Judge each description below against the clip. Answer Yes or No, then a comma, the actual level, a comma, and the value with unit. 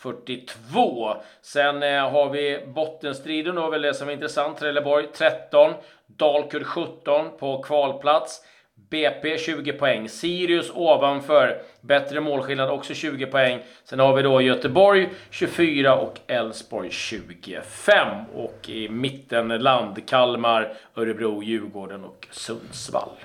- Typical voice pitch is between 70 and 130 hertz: No, medium, 140 Hz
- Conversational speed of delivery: No, slow, 115 wpm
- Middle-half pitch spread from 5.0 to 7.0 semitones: No, average, 3.4 semitones